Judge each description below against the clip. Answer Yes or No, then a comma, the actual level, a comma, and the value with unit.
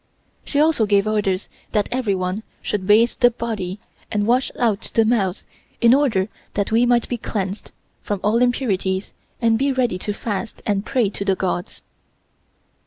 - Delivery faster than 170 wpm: No, average, 165 wpm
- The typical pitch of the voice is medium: No, high, 215 Hz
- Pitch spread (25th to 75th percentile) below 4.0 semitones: Yes, average, 3.5 semitones